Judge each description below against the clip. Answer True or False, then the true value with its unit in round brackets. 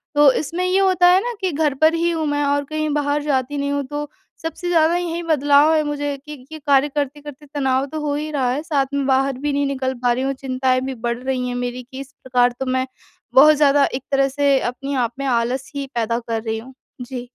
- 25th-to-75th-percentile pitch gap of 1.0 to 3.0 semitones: True (2.4 semitones)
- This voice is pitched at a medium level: False (280 Hz)